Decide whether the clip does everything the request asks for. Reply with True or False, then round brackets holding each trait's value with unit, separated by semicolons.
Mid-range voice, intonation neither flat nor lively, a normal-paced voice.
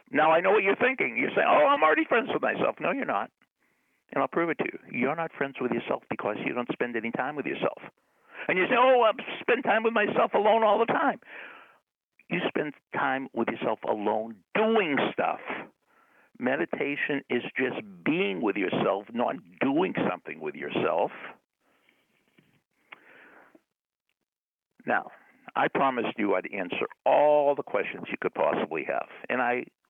False (165 Hz; 8.5 semitones; 165 wpm)